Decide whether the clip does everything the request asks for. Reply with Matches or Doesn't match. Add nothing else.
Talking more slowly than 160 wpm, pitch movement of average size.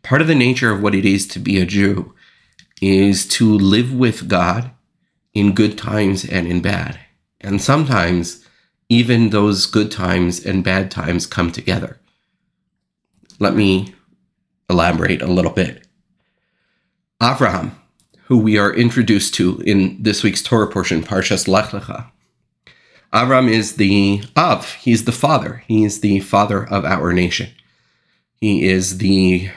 Matches